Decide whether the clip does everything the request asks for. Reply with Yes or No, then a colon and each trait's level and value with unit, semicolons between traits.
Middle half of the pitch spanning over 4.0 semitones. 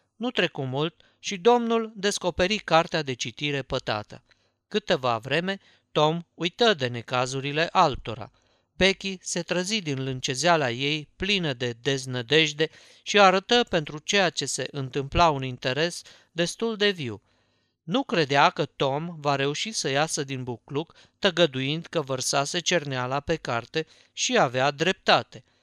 Yes: wide, 5.4 semitones